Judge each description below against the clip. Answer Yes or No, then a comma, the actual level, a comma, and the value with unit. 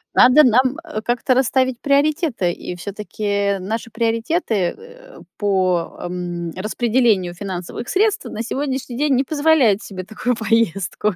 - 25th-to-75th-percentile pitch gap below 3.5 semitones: No, average, 5.1 semitones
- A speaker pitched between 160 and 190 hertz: No, high, 230 Hz